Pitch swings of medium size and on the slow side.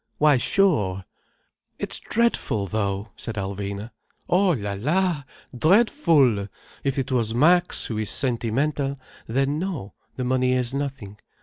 No: wide, 6.2 semitones; slow, 125 wpm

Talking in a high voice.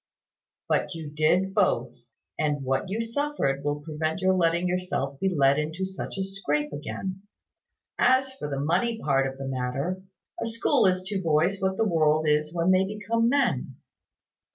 No: medium, 170 Hz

